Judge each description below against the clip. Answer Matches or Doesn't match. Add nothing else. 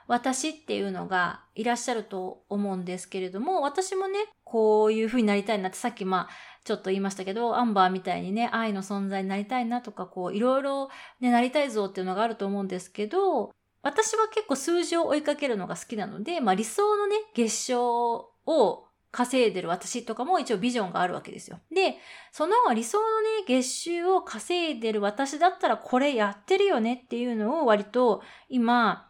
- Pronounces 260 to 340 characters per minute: Doesn't match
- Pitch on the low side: Doesn't match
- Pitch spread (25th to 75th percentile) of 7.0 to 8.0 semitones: Matches